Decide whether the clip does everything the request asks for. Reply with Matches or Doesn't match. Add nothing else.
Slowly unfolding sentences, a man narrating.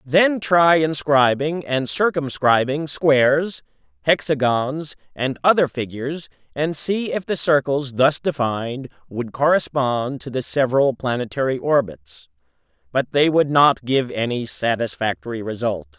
Matches